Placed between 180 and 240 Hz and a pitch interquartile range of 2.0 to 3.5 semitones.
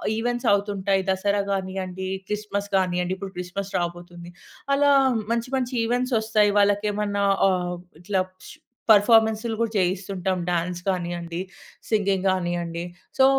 Yes: high, 195 Hz; average, 2.8 semitones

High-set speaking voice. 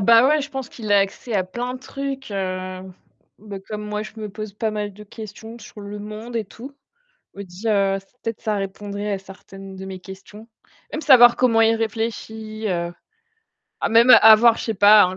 Yes: high, 215 Hz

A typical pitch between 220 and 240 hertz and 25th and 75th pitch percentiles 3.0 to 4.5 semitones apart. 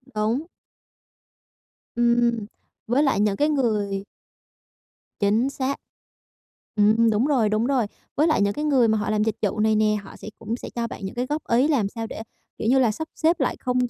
Yes: high, 230 Hz; average, 3.8 semitones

